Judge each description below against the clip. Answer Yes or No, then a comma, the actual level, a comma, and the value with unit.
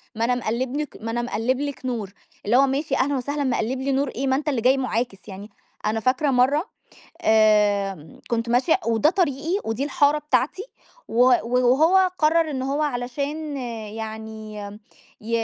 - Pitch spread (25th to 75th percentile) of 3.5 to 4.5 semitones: Yes, average, 4.1 semitones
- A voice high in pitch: Yes, very high, 255 Hz